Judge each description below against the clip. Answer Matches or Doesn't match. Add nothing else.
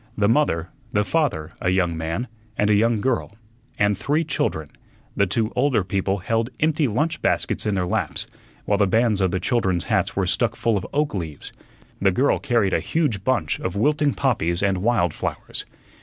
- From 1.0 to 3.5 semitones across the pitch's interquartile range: Doesn't match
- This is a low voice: Matches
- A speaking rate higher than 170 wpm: Matches